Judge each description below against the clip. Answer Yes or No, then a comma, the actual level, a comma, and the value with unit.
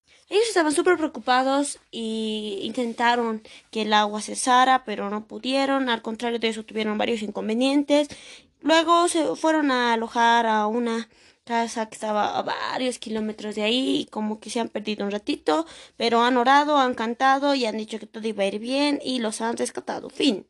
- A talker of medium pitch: No, high, 235 Hz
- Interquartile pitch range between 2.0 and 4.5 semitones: Yes, average, 3.8 semitones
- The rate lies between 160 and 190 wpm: Yes, average, 180 wpm